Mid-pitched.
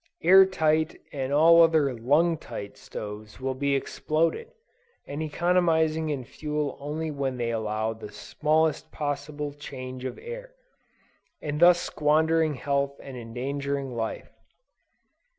Yes: medium, 145 Hz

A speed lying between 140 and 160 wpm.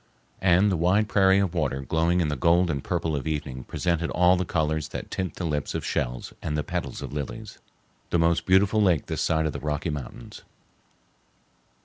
No: average, 195 wpm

